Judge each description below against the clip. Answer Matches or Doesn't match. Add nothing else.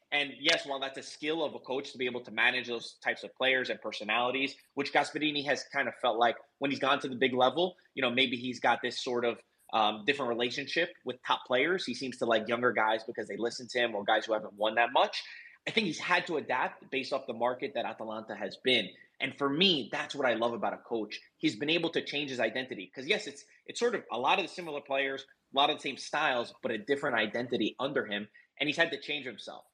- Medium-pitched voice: Doesn't match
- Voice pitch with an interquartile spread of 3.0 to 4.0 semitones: Matches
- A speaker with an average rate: Doesn't match